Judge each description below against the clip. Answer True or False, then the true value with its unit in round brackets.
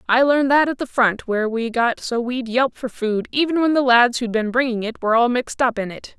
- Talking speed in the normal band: False (270 wpm)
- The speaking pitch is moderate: False (245 Hz)